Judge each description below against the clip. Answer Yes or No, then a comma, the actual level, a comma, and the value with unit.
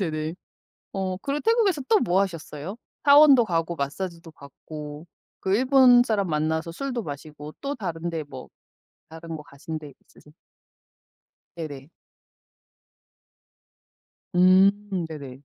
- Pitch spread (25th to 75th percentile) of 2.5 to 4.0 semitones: No, average, 5.2 semitones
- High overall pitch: No, medium, 170 Hz